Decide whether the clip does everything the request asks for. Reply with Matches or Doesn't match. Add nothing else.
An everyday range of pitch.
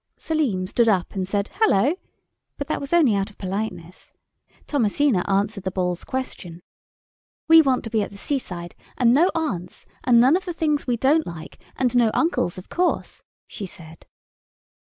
Doesn't match